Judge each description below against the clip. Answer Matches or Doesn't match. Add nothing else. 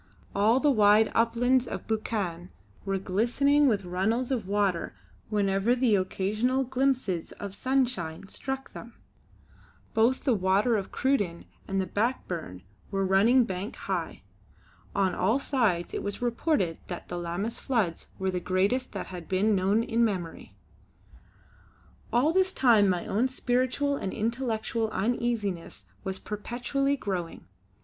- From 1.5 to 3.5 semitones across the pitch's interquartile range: Doesn't match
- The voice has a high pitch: Matches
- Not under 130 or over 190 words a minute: Matches